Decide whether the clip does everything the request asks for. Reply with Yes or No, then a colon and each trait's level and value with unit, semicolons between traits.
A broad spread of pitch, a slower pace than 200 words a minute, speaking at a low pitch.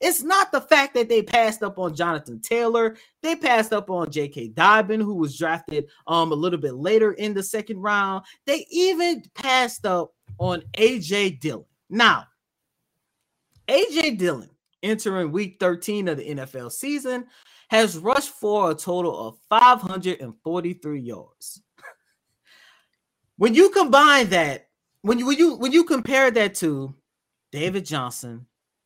No: wide, 7.2 semitones; average, 145 wpm; high, 200 Hz